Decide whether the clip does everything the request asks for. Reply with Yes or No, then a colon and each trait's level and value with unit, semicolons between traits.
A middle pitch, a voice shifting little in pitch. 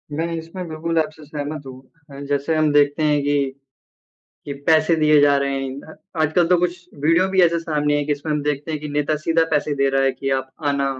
Yes: medium, 150 Hz; narrow, 2.2 semitones